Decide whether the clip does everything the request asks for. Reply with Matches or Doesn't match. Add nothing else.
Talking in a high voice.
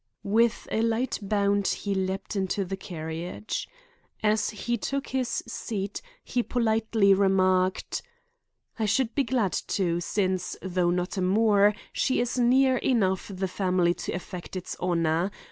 Matches